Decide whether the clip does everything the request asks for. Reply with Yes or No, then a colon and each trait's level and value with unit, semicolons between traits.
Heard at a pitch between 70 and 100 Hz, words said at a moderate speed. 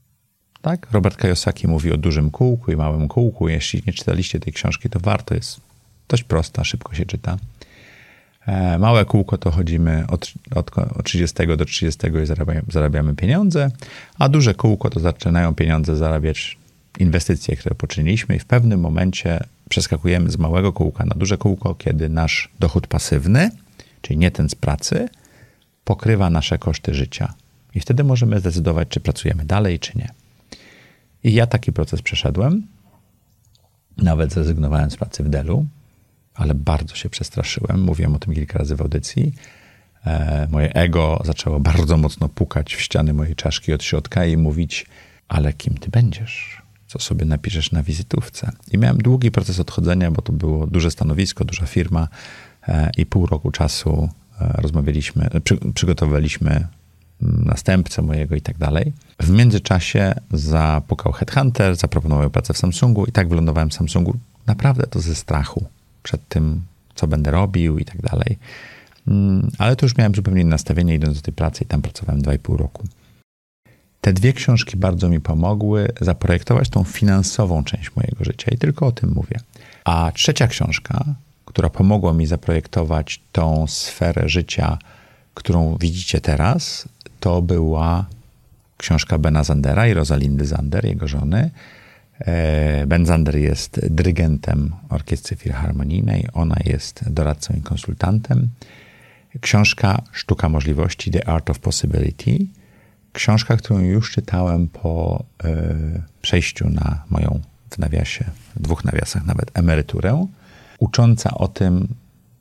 Yes: very low, 90 Hz; average, 140 wpm